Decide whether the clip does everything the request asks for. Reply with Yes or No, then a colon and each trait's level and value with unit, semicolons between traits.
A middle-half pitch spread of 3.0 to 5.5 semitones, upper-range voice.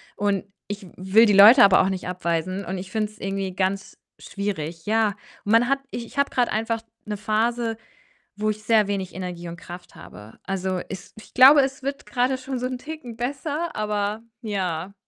Yes: average, 4.1 semitones; high, 210 Hz